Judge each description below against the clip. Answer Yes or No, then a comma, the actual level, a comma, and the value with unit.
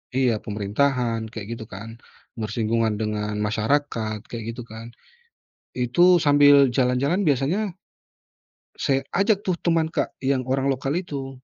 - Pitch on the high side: No, low, 130 Hz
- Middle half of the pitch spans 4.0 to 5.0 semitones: Yes, average, 4.4 semitones